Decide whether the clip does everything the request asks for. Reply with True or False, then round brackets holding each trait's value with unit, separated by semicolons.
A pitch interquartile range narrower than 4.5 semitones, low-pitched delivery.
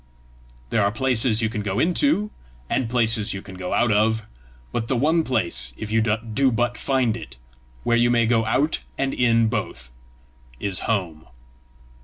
True (2.8 semitones; 115 Hz)